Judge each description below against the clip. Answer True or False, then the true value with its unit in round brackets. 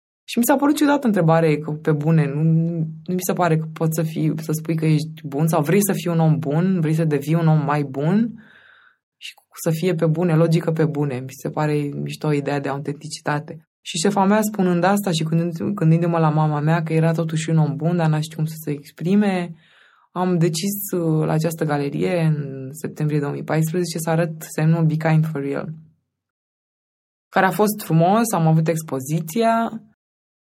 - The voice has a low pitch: False (165 Hz)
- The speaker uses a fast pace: True (205 wpm)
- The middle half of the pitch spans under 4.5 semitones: True (2.4 semitones)